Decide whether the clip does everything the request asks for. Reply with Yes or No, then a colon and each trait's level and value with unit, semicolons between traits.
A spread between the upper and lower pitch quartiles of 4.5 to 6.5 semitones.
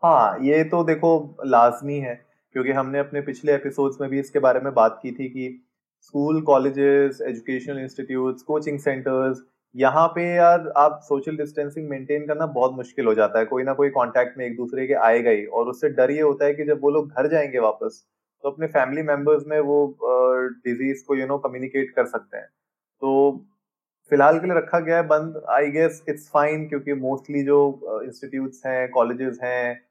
No: narrow, 2.5 semitones